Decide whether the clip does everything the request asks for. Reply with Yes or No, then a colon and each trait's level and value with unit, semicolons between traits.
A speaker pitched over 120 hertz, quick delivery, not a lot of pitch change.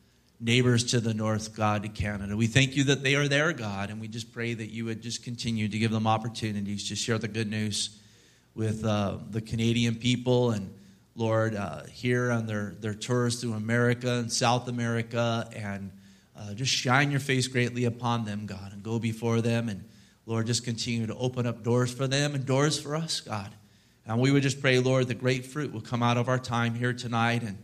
No: low, 115 Hz; fast, 215 wpm; narrow, 2.3 semitones